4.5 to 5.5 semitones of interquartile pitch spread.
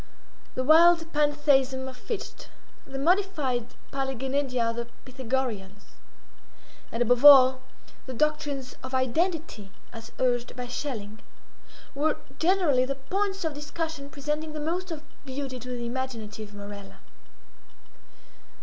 No: average, 3.6 semitones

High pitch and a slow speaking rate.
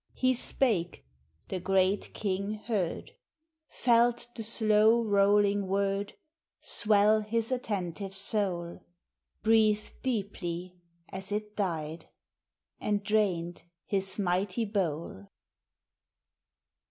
Yes: high, 200 Hz; slow, 90 wpm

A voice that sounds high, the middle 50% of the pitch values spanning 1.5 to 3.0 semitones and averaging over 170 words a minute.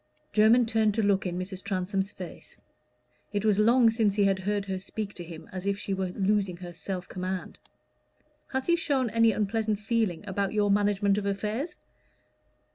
Yes: high, 200 Hz; narrow, 2.4 semitones; average, 180 wpm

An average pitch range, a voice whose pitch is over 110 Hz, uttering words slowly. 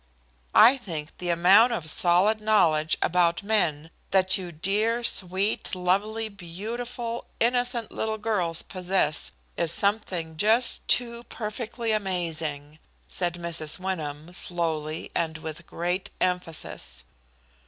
Yes: average, 4.8 semitones; medium, 185 Hz; slow, 110 wpm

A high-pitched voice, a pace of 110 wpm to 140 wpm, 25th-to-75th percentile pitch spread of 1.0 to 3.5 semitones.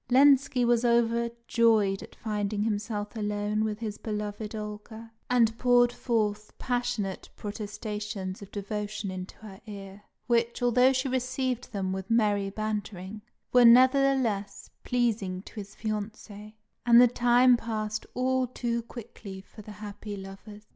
Yes: high, 215 Hz; slow, 135 wpm; narrow, 2.6 semitones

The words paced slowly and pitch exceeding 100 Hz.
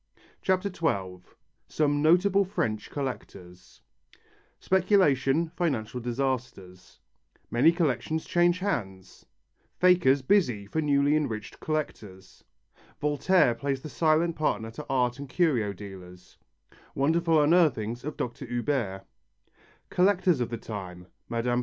Yes: slow, 110 wpm; low, 135 Hz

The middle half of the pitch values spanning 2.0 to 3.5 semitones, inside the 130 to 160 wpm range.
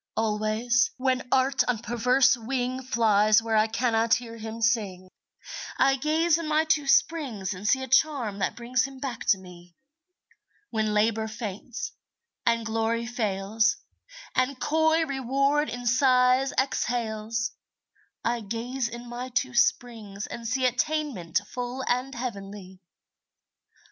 Yes: average, 3.1 semitones; slow, 135 wpm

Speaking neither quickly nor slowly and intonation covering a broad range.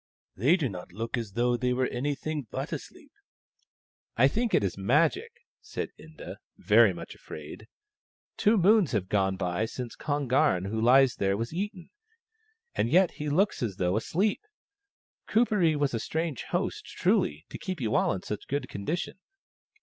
Yes: average, 175 wpm; wide, 7.8 semitones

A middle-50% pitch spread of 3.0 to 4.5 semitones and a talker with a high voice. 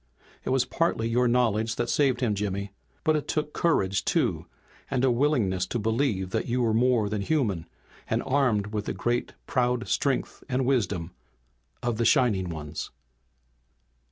No: average, 4.1 semitones; low, 120 Hz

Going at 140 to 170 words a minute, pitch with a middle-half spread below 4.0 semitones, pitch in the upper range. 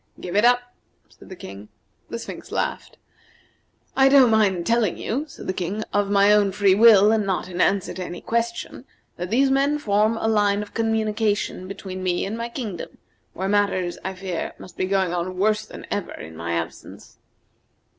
No: average, 185 wpm; average, 3.3 semitones; high, 205 Hz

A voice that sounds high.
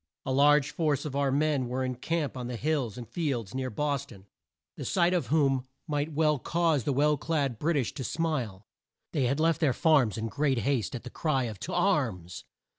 No: medium, 140 Hz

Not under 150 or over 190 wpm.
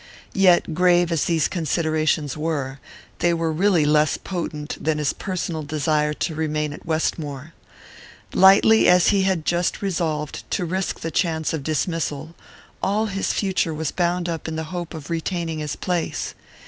Yes: average, 160 wpm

